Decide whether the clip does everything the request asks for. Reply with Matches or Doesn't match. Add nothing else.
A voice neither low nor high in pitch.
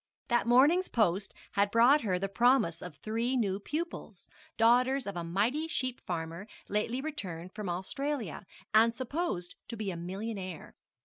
Doesn't match